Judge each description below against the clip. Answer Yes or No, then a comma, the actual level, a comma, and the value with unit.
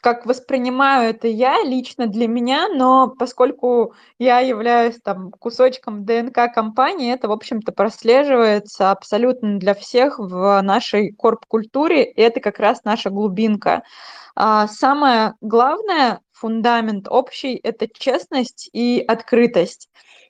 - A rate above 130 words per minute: No, average, 115 wpm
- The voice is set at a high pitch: Yes, high, 235 Hz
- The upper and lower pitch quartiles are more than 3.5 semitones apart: No, average, 2.9 semitones